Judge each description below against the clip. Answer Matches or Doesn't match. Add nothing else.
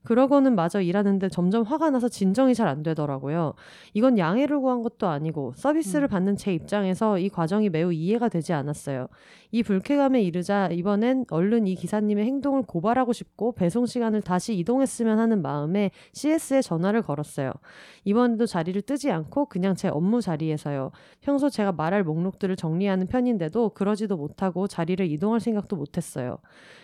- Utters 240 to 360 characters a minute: Doesn't match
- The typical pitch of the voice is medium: Doesn't match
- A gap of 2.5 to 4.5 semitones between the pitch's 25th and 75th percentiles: Doesn't match